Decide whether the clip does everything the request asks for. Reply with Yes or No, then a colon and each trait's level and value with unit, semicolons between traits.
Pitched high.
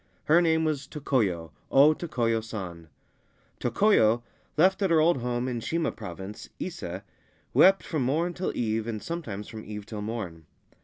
No: low, 120 Hz